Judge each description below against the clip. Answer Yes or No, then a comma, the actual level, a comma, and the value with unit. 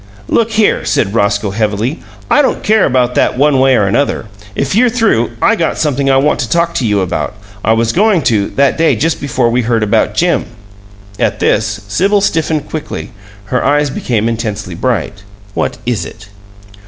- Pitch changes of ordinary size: No, wide, 6.7 semitones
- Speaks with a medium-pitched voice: No, low, 125 Hz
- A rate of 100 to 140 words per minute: No, average, 185 wpm